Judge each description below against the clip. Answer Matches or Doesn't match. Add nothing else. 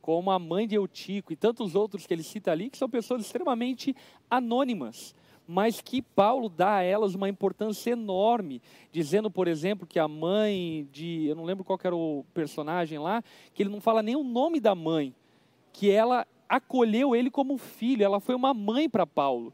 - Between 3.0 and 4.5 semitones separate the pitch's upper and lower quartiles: Doesn't match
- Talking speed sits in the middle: Doesn't match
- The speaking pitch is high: Matches